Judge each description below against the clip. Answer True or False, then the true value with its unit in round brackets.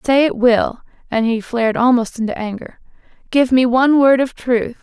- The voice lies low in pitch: False (245 Hz)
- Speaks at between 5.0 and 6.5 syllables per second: True (5.1 syllables/s)